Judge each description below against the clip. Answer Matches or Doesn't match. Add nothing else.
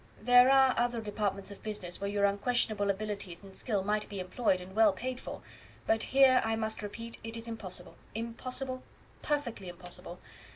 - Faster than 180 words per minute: Doesn't match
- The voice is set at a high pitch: Matches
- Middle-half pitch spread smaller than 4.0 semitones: Matches